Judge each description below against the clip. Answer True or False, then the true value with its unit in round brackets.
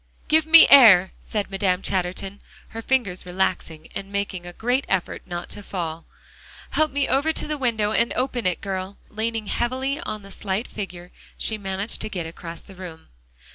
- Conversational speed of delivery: True (180 wpm)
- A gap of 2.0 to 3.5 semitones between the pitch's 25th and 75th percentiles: False (4.6 semitones)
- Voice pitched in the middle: False (200 Hz)